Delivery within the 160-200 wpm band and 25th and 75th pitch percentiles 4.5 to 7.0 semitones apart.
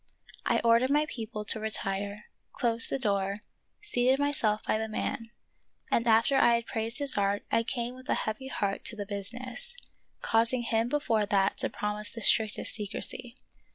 No: average, 170 wpm; average, 2.8 semitones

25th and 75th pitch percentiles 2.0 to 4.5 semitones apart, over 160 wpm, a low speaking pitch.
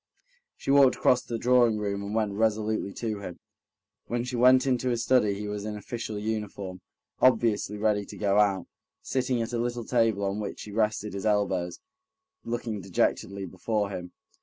Yes: average, 2.8 semitones; average, 175 wpm; low, 105 Hz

